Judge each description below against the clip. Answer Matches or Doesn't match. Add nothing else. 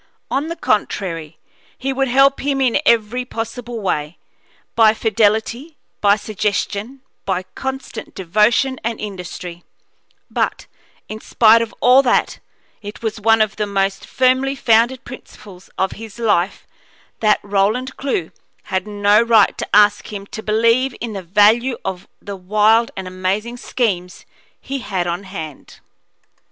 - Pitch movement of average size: Matches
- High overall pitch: Matches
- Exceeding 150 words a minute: Doesn't match